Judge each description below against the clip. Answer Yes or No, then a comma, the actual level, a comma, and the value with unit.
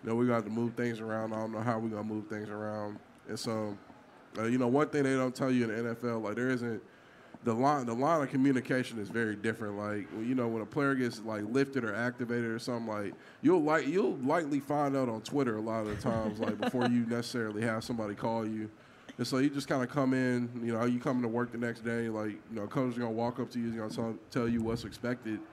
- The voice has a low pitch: Yes, low, 115 Hz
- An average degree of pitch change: No, narrow, 2.3 semitones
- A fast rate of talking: Yes, fast, 265 wpm